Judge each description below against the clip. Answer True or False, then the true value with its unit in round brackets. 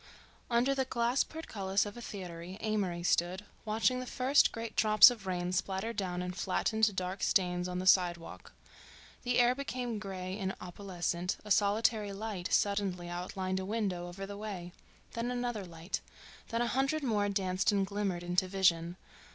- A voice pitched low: False (195 Hz)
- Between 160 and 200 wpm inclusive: True (165 wpm)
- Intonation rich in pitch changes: False (3.8 semitones)